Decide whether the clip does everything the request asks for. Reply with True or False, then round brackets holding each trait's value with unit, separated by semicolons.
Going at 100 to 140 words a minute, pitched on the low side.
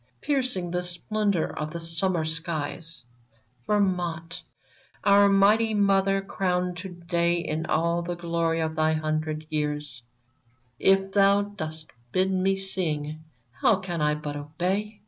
False (135 wpm; 170 Hz)